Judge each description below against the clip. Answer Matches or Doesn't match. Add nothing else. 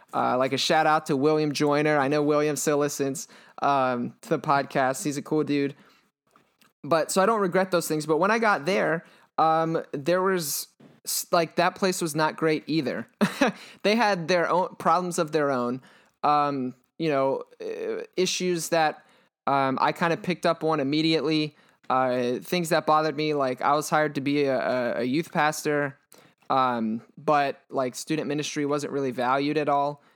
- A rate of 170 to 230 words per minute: Matches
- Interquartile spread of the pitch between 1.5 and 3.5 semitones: Matches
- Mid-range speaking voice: Matches